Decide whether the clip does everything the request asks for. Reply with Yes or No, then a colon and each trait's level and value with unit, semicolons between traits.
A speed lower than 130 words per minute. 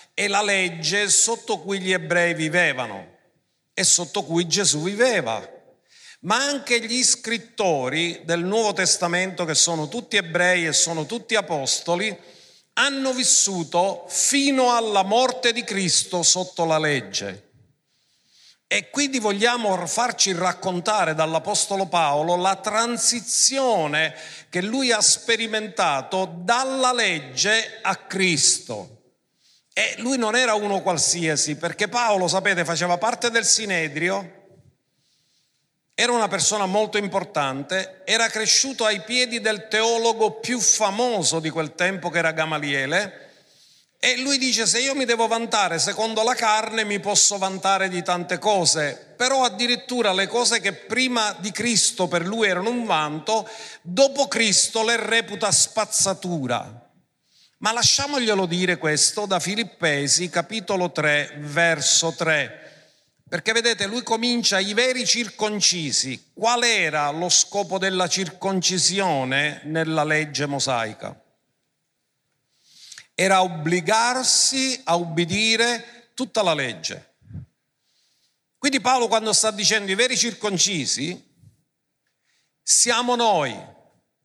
Yes: average, 120 wpm